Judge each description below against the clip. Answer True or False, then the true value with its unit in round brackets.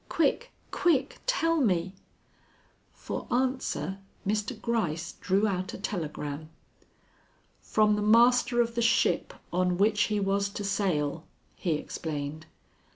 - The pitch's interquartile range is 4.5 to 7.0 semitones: True (5.2 semitones)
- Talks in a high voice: True (205 Hz)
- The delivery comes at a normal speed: False (120 wpm)